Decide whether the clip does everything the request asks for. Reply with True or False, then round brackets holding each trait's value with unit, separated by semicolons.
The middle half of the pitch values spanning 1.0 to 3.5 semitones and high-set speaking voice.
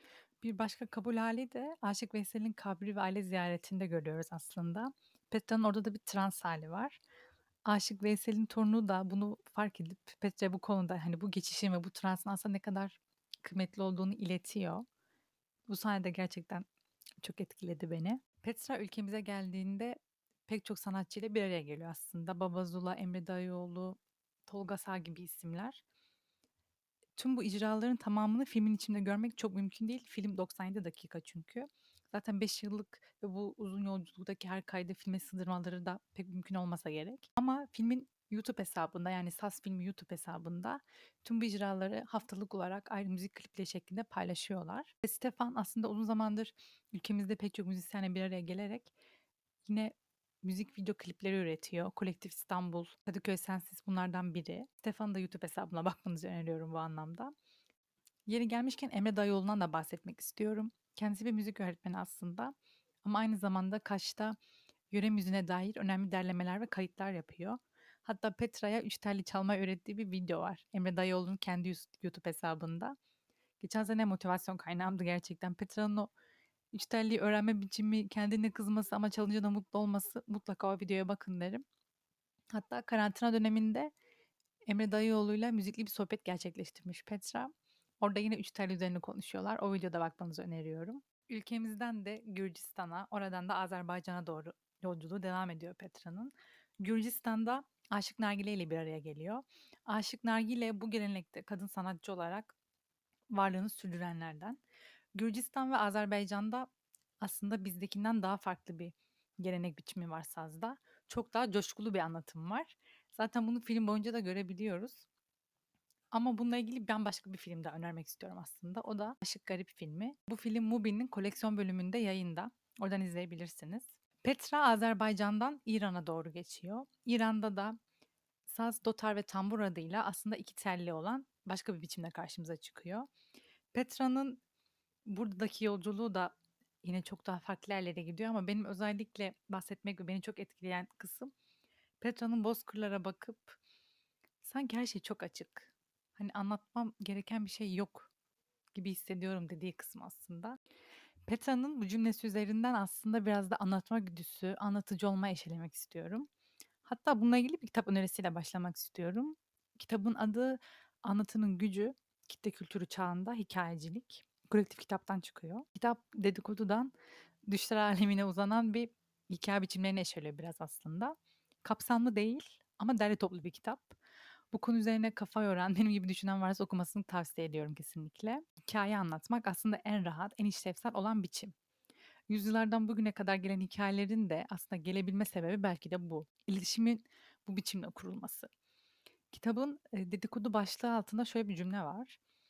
True (3.2 semitones; 205 Hz)